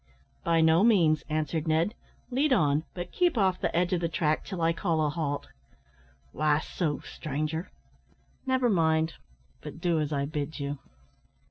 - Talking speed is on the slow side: No, average, 160 wpm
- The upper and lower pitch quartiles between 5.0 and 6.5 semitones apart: No, narrow, 2.6 semitones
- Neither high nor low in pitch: Yes, medium, 160 Hz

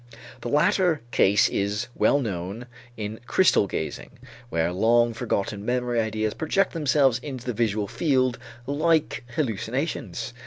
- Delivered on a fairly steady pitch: No, average, 5.1 semitones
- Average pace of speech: No, slow, 125 wpm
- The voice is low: Yes, low, 120 Hz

